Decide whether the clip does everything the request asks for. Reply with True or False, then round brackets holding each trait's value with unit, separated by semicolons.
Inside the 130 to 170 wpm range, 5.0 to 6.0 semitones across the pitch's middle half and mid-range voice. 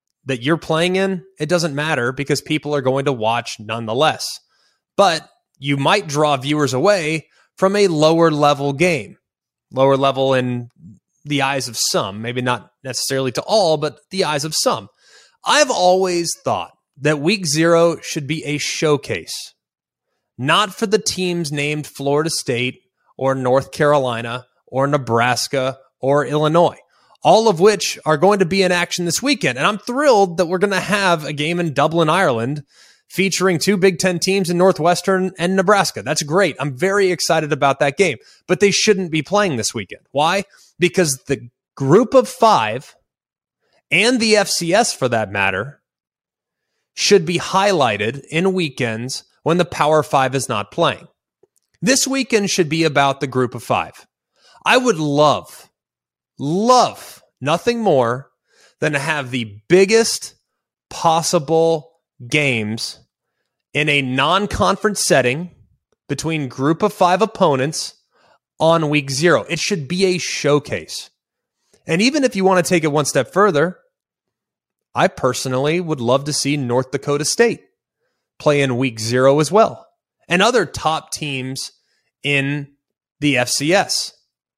True (150 wpm; 5.4 semitones; 155 Hz)